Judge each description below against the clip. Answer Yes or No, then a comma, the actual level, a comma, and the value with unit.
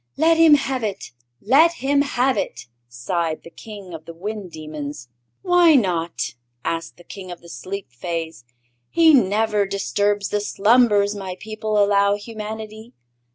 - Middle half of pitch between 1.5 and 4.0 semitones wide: No, average, 5.1 semitones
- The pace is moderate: Yes, average, 150 wpm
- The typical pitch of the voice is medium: No, high, 205 Hz